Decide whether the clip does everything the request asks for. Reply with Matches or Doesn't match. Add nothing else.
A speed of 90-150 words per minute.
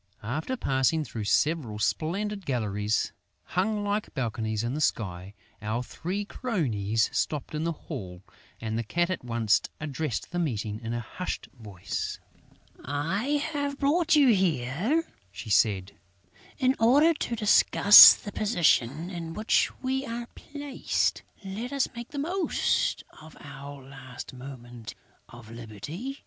Matches